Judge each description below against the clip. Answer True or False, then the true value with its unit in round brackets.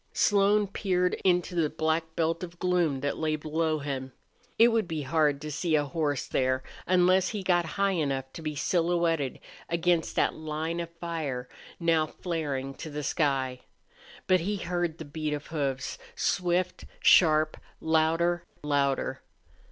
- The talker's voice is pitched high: False (160 Hz)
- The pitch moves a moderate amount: True (3.0 semitones)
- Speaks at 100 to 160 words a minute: True (150 wpm)